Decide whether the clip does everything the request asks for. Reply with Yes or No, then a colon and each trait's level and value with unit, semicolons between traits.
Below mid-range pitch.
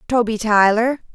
No: high, 225 Hz